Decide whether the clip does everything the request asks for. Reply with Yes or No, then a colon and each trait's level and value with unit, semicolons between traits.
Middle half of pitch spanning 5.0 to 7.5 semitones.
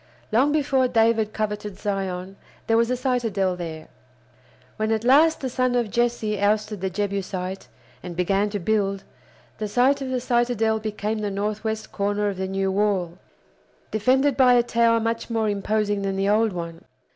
No: average, 3.2 semitones